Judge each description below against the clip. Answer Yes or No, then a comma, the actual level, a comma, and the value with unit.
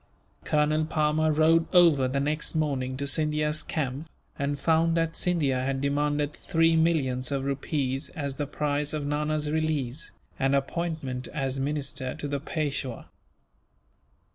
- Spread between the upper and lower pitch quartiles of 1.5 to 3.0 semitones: Yes, narrow, 2.4 semitones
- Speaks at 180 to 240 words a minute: No, average, 140 wpm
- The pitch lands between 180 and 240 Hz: No, medium, 150 Hz